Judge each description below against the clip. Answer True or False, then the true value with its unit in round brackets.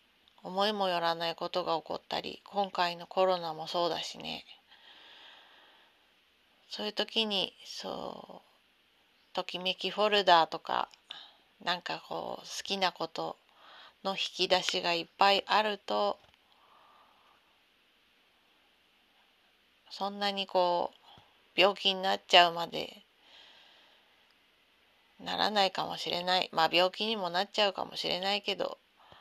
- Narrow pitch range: True (2.3 semitones)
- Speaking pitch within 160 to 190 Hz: True (185 Hz)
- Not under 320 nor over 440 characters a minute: False (235 characters per minute)